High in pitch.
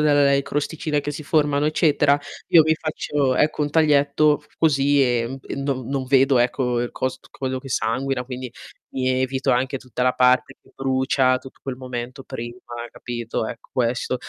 No: low, 135 Hz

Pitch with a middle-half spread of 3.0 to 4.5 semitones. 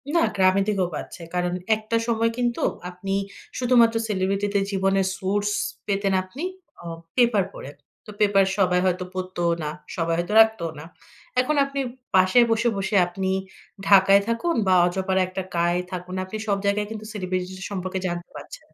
No: narrow, 2.5 semitones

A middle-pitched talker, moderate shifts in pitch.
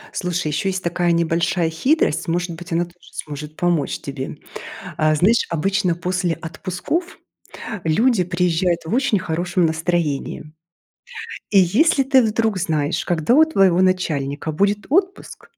Yes: medium, 175 Hz; average, 3.3 semitones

